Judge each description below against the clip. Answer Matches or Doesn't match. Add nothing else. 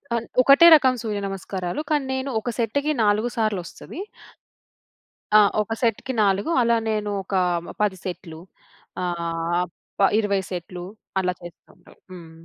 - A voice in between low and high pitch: Doesn't match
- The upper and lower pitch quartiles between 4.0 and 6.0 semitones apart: Matches